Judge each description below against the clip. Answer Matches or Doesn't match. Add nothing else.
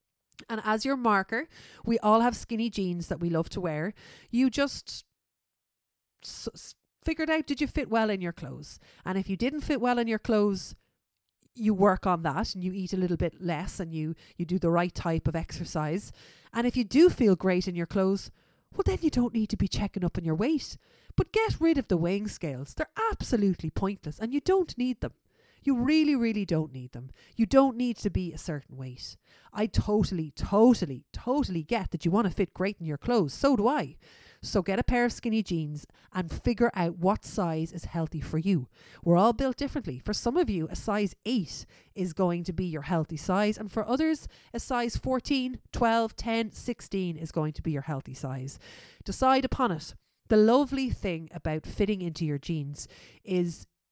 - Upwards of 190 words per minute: Matches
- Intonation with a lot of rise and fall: Matches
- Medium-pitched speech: Doesn't match